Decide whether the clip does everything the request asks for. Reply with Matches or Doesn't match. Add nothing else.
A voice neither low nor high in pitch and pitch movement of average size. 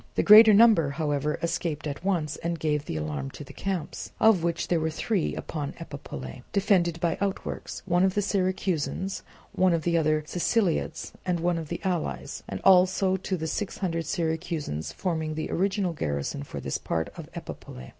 Matches